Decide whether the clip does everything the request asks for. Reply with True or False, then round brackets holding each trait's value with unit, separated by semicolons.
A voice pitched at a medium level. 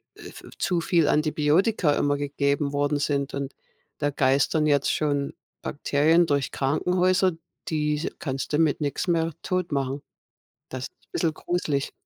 True (150 Hz)